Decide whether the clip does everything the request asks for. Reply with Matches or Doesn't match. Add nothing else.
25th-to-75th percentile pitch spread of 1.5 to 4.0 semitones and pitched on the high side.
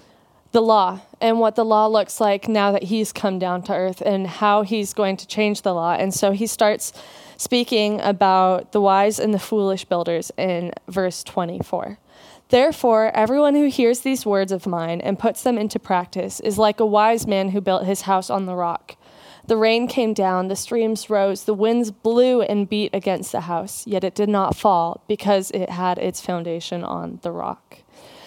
Matches